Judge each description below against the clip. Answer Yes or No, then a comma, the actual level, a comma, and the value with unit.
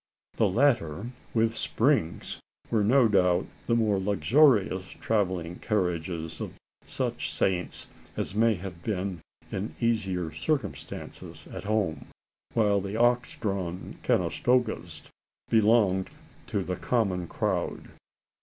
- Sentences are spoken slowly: Yes, slow, 110 wpm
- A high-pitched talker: No, low, 100 Hz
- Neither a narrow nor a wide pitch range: Yes, average, 4.1 semitones